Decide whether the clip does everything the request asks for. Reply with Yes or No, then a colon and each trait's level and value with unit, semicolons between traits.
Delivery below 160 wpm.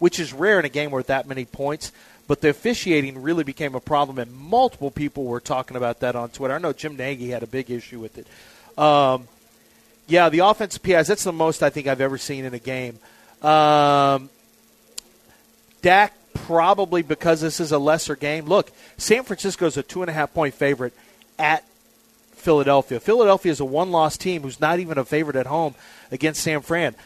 No: average, 195 wpm